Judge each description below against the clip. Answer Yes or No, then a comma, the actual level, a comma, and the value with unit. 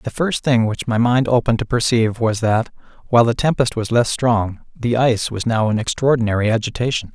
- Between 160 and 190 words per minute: No, average, 200 wpm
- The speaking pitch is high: No, low, 115 Hz